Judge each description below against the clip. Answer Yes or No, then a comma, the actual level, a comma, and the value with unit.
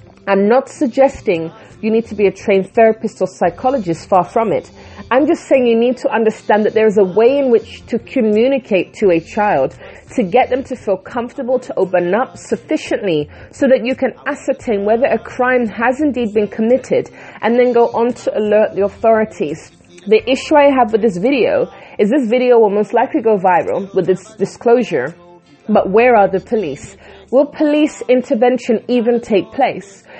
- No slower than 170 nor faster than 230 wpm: Yes, average, 185 wpm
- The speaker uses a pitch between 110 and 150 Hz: No, high, 230 Hz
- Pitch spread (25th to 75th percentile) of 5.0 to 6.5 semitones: No, average, 3.8 semitones